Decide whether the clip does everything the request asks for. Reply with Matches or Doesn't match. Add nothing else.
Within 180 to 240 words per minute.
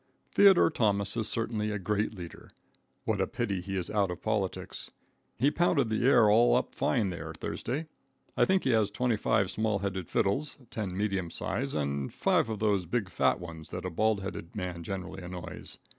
Matches